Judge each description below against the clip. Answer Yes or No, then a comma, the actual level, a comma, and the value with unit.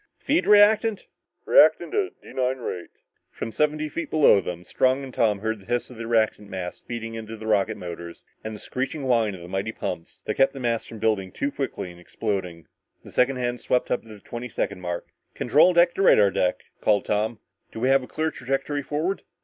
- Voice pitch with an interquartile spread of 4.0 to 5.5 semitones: Yes, average, 5.1 semitones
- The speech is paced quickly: Yes, fast, 215 wpm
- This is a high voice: No, low, 115 Hz